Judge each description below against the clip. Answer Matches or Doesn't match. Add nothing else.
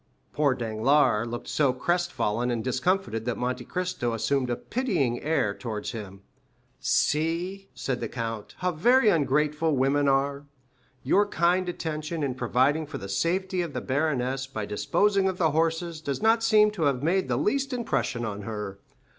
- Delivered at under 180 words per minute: Matches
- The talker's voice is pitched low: Doesn't match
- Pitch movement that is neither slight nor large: Doesn't match